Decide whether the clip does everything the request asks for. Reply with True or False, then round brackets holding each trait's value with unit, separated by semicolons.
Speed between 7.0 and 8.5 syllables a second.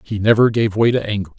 False (6.5 syllables/s)